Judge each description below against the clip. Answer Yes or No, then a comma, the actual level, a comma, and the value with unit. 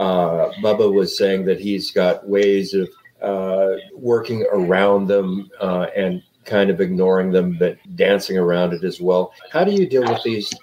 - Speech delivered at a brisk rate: No, average, 175 wpm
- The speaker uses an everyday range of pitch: No, narrow, 1.4 semitones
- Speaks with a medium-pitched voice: No, very low, 95 Hz